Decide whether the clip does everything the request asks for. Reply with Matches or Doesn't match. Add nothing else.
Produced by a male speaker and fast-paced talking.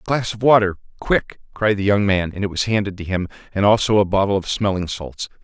Matches